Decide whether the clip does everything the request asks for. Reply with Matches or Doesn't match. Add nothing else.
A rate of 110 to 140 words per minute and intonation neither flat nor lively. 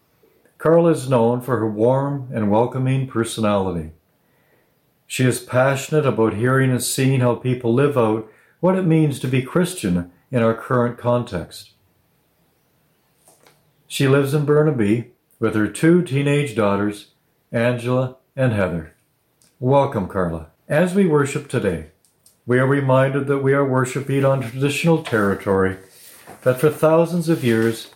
Matches